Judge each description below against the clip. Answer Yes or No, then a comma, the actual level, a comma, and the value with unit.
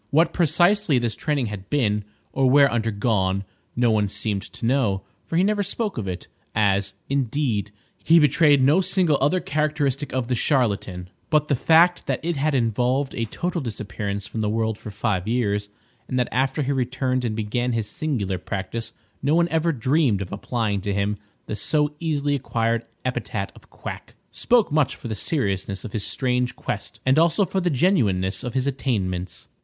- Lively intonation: Yes, wide, 6.1 semitones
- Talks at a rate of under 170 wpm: No, average, 175 wpm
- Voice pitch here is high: No, low, 125 Hz